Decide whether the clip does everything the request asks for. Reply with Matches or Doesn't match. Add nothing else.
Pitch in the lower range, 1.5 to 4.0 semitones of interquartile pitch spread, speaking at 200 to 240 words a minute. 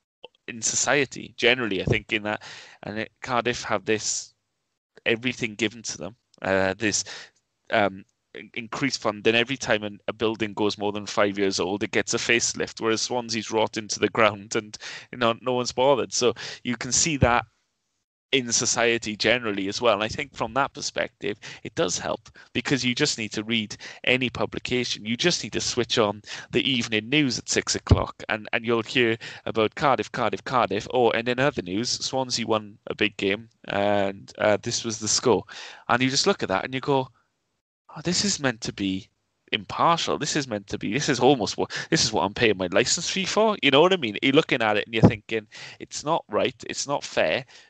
Matches